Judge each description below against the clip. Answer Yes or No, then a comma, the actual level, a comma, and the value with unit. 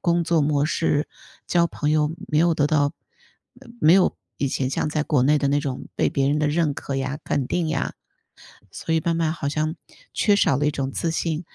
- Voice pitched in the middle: Yes, medium, 150 Hz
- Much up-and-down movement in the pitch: No, narrow, 2.4 semitones